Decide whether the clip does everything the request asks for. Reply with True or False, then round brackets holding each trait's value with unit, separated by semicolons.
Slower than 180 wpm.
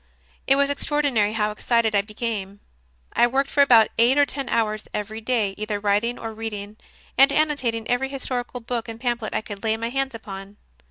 False (185 wpm)